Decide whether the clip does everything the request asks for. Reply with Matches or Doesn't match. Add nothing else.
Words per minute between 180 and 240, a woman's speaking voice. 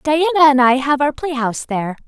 Matches